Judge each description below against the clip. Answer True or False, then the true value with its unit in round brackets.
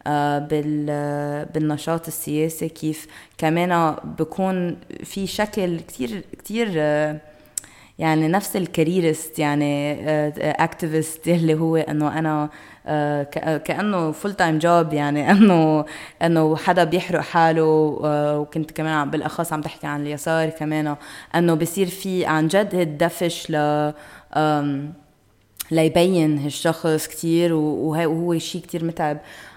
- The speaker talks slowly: False (100 wpm)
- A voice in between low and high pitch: True (155 Hz)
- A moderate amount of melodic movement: False (2.1 semitones)